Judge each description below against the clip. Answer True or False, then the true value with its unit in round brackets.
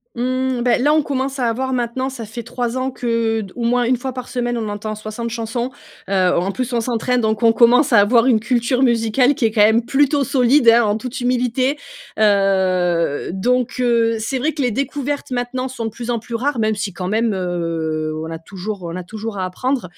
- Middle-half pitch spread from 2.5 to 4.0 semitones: True (2.9 semitones)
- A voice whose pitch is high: True (235 Hz)